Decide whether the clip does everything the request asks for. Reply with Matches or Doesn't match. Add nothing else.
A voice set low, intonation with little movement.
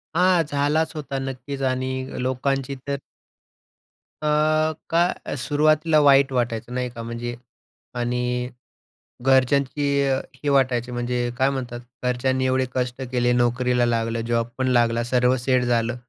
Matches